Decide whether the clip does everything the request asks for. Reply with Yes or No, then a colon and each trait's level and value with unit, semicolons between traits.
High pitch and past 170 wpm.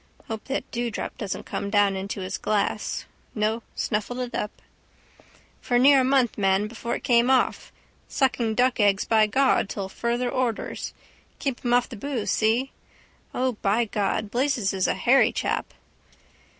No: high, 235 Hz; average, 160 wpm